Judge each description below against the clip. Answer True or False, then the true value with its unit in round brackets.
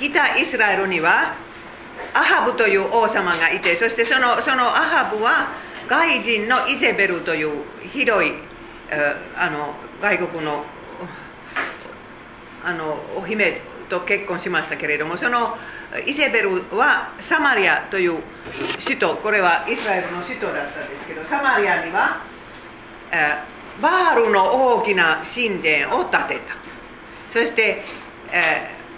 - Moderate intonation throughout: False (6.5 semitones)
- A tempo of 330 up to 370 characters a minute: False (260 characters per minute)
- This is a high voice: True (205 Hz)